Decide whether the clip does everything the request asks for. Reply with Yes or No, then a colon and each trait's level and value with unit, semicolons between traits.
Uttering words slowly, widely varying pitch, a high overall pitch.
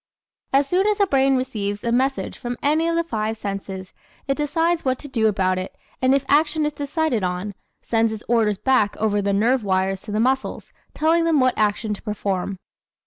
No: average, 200 wpm; wide, 5.8 semitones; high, 240 Hz